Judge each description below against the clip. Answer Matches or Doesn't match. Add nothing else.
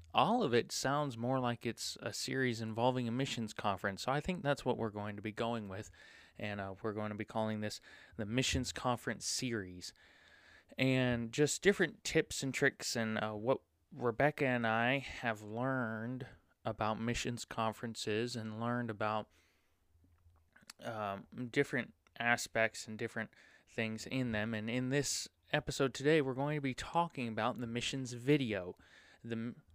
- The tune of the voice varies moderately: Matches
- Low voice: Matches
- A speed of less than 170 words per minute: Matches